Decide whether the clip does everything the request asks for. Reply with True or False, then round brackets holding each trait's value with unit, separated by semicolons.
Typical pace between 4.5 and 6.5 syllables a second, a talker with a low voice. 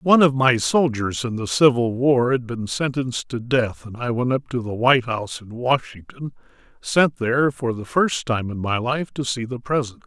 True (5.0 syllables/s; 125 Hz)